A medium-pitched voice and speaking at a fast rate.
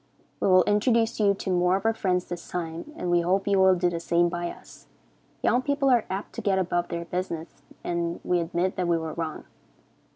Yes: medium, 180 Hz; fast, 220 wpm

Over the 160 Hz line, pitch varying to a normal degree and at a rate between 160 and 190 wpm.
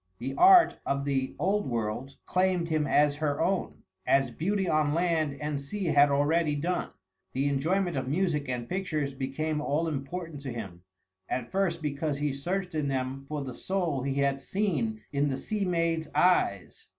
No: medium, 150 Hz; average, 4.1 semitones; average, 175 wpm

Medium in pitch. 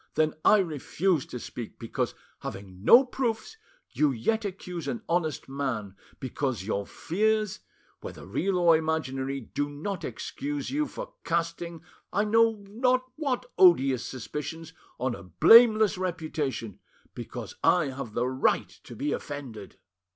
Yes: medium, 160 Hz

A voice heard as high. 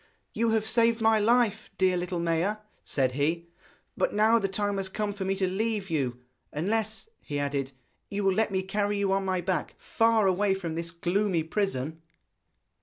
Yes: high, 195 Hz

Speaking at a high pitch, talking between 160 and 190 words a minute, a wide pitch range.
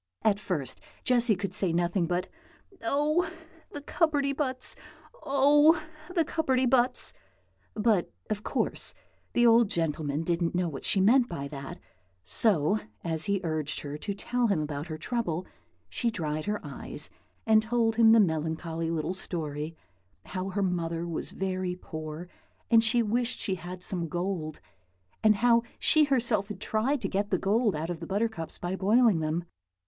Yes: high, 195 Hz; average, 165 wpm; wide, 5.9 semitones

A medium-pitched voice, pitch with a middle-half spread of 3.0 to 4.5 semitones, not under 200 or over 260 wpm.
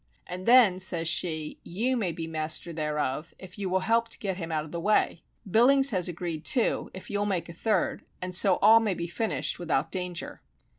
Yes: medium, 180 Hz; average, 3.9 semitones; fast, 205 wpm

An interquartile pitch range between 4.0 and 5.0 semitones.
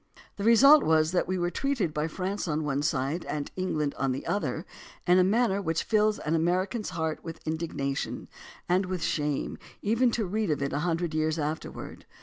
Yes: average, 4.5 semitones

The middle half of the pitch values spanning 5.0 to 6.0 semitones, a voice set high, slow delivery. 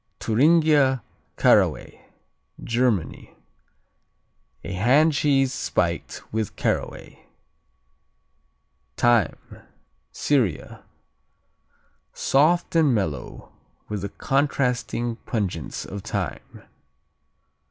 No: wide, 5.4 semitones; low, 125 Hz; slow, 70 wpm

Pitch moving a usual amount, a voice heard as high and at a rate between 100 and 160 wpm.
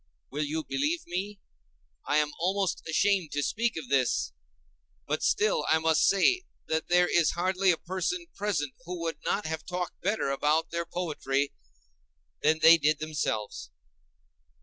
No: average, 3.9 semitones; medium, 165 Hz; average, 150 wpm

